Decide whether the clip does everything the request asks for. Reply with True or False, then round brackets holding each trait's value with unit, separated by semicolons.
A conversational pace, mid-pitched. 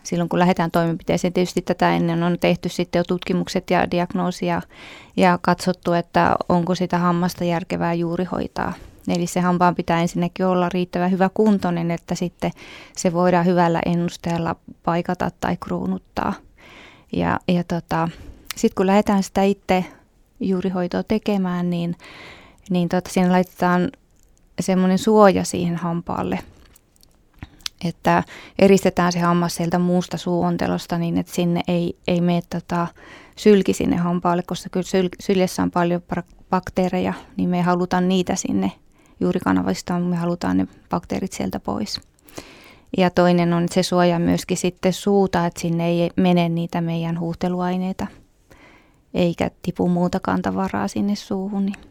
True (140 wpm; 180 Hz)